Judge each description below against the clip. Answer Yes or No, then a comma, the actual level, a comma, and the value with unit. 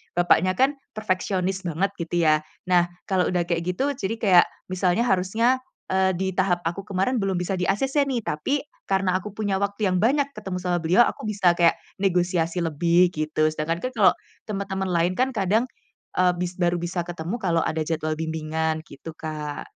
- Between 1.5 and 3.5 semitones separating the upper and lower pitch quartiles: Yes, average, 2.8 semitones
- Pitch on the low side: No, medium, 180 Hz